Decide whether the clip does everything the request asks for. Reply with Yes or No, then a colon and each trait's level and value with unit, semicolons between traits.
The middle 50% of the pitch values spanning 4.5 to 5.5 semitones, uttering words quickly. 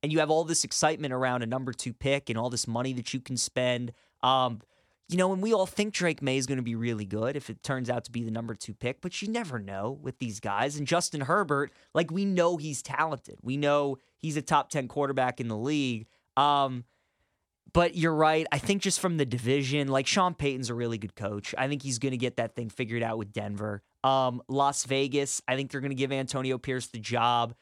No: average, 3.3 semitones; fast, 240 wpm